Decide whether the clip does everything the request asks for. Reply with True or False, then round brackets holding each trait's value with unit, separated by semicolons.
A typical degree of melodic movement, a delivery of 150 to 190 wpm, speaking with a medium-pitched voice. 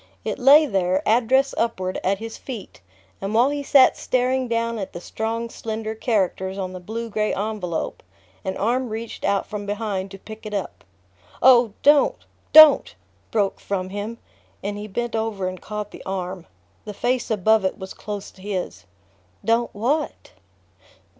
False (3.1 semitones; 165 wpm; 215 Hz)